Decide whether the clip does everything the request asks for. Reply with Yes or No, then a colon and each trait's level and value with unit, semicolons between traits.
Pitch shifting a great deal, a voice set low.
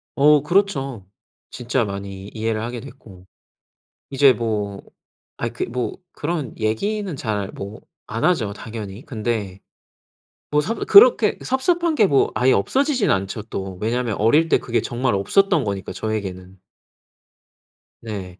Yes: wide, 6.7 semitones; low, 115 Hz